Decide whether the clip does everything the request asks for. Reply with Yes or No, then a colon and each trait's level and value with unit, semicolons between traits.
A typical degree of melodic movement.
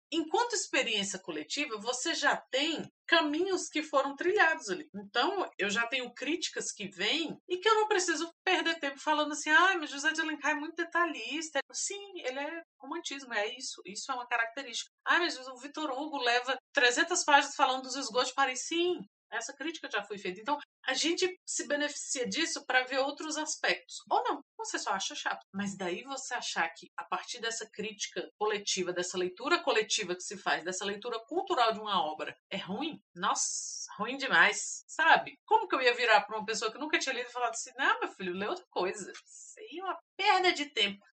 No: wide, 6.7 semitones